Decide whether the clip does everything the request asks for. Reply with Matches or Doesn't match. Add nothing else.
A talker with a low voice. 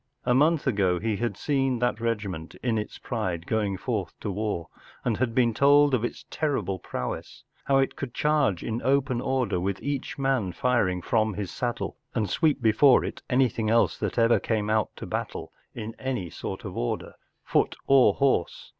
Matches